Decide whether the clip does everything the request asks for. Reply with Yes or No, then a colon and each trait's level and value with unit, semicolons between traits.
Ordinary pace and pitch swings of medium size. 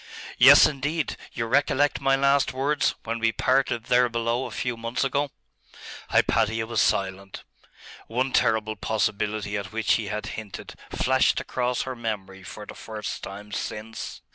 Yes: average, 150 wpm; average, 3.5 semitones